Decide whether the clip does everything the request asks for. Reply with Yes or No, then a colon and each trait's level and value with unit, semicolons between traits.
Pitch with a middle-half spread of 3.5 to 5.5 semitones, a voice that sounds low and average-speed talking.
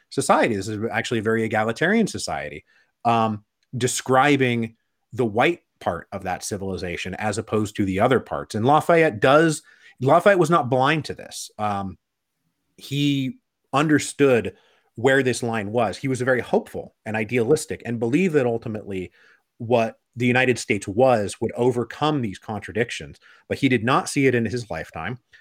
Yes: average, 3.8 semitones; low, 120 Hz; average, 160 wpm